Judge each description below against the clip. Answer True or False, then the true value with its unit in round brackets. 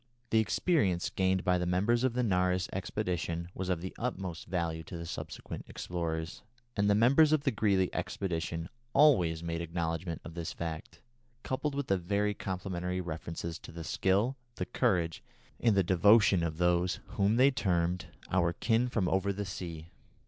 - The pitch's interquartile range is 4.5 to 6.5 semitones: False (3.4 semitones)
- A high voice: False (90 Hz)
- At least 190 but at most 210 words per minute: False (165 wpm)